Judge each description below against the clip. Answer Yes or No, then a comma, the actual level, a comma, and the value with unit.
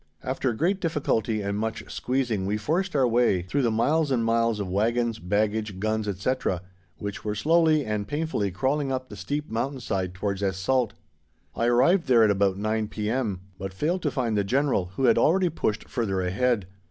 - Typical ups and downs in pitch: Yes, average, 4.7 semitones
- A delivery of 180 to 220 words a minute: Yes, average, 190 wpm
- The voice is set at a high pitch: No, low, 115 Hz